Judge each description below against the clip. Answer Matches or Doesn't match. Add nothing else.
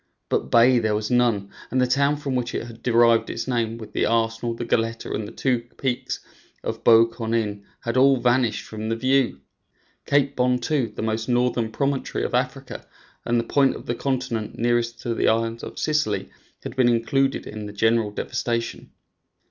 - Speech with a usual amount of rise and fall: Doesn't match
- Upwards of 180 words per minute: Matches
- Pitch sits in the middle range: Doesn't match